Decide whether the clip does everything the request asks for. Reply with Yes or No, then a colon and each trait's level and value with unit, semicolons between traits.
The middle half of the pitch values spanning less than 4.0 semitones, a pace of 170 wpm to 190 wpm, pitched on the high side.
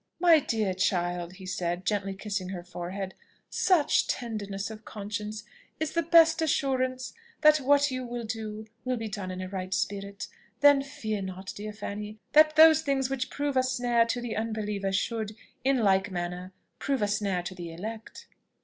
No: average, 5.1 semitones; average, 175 wpm; high, 215 Hz